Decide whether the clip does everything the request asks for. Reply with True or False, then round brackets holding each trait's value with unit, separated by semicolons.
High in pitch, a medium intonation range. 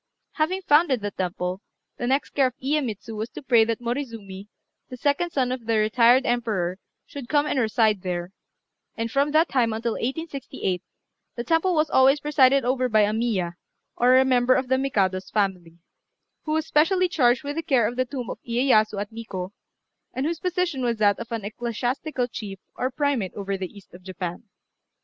True (240 Hz; 4.7 semitones)